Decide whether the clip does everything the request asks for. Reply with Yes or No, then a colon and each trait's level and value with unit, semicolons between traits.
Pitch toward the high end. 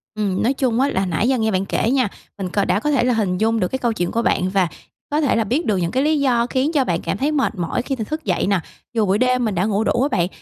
Yes: high, 225 Hz